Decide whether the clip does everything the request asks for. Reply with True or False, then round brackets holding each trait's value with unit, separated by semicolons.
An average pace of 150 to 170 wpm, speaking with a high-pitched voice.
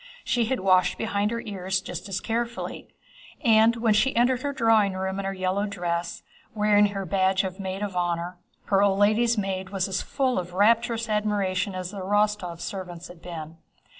False (185 wpm; 200 Hz)